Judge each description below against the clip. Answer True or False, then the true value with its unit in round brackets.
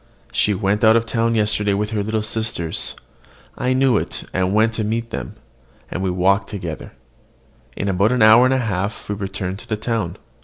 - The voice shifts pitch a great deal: False (2.7 semitones)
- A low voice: True (105 Hz)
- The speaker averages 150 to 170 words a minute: False (185 wpm)